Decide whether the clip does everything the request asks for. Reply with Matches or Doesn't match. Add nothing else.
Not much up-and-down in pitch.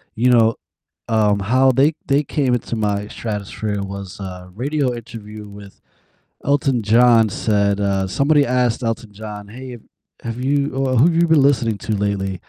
Doesn't match